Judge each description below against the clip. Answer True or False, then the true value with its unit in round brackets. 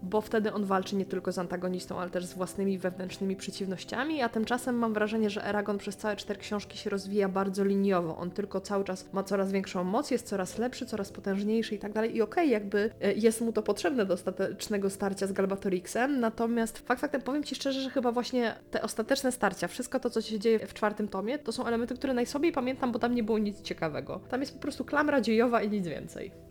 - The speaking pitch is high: True (210 Hz)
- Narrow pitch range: False (3.6 semitones)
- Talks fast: True (225 wpm)